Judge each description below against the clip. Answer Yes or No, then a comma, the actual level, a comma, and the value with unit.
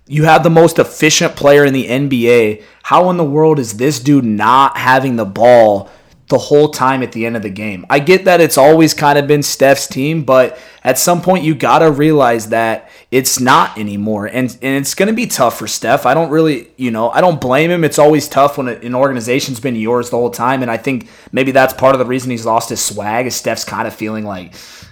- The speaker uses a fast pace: Yes, fast, 235 wpm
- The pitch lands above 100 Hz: Yes, low, 130 Hz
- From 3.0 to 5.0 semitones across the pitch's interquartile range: Yes, average, 4.2 semitones